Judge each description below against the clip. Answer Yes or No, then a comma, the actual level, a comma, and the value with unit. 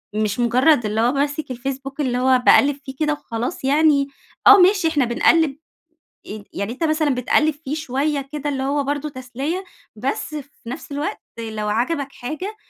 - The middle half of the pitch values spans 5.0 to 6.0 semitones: No, average, 3.5 semitones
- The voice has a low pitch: No, very high, 275 Hz